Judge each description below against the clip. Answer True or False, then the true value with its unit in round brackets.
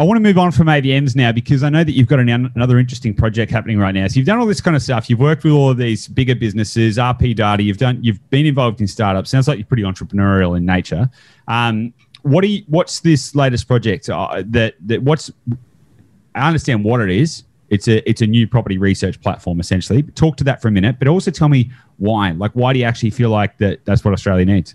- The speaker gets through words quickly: True (245 wpm)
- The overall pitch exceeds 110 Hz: True (120 Hz)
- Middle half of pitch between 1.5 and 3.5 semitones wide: False (4.6 semitones)